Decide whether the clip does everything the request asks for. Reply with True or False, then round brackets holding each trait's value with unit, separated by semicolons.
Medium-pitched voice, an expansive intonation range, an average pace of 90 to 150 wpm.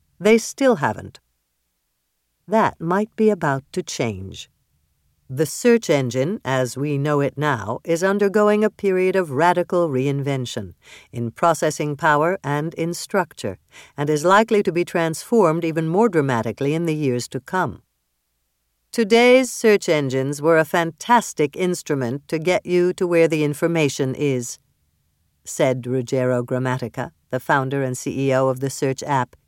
True (145 Hz; 5.7 semitones; 140 wpm)